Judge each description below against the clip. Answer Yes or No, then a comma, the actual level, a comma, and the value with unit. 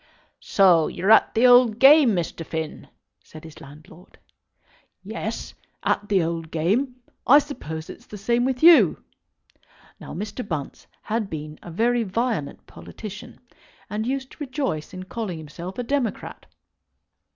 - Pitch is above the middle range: Yes, high, 205 Hz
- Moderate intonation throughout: No, wide, 7.0 semitones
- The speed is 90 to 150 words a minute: Yes, average, 140 wpm